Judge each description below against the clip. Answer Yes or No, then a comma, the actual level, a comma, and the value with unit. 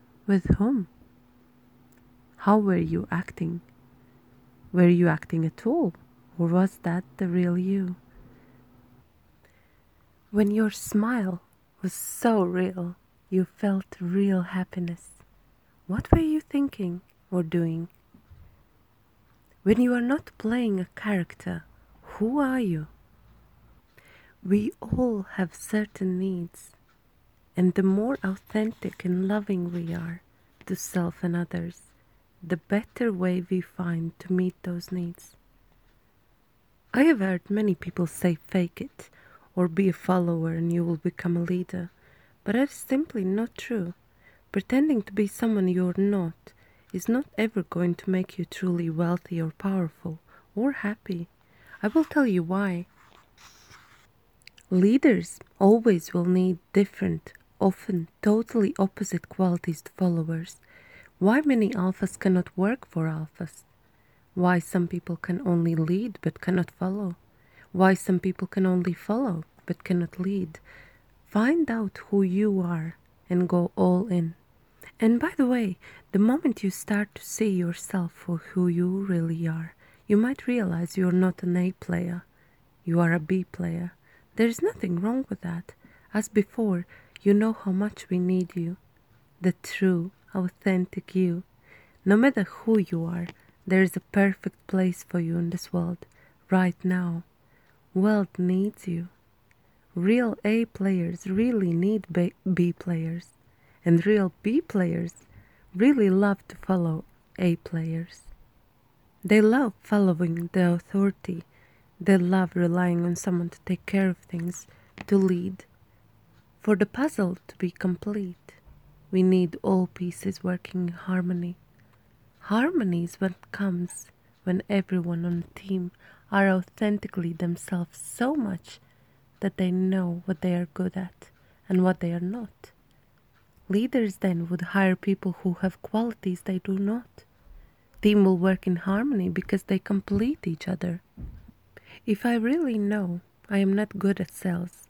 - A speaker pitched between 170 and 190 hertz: Yes, medium, 185 Hz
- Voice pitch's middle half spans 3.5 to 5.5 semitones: No, narrow, 2.6 semitones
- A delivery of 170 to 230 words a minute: No, average, 140 wpm